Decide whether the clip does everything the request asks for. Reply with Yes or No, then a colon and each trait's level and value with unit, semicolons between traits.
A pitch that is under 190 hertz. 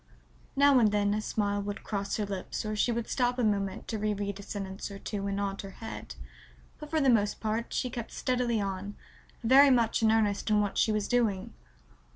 No: high, 210 Hz